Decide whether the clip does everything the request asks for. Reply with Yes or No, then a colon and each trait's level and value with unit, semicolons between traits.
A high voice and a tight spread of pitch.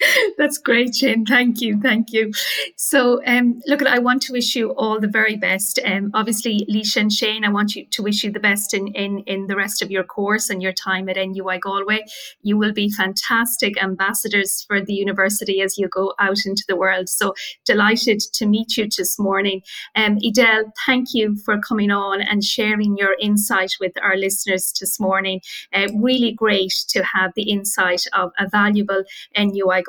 Yes: high, 205 Hz; narrow, 2.3 semitones